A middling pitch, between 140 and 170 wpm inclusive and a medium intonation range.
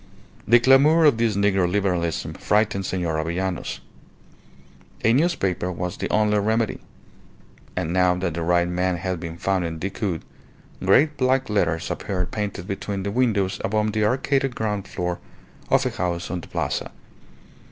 No: very low, 95 Hz; average, 150 wpm; average, 3.5 semitones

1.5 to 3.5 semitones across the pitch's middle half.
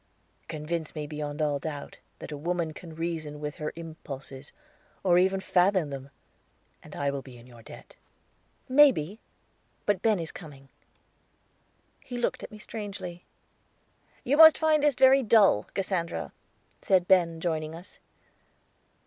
No: average, 4.8 semitones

